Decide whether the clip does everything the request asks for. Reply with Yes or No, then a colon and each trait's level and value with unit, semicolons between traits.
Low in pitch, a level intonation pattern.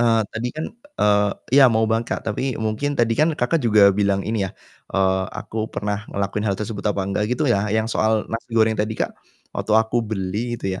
Yes: low, 110 Hz; narrow, 2.1 semitones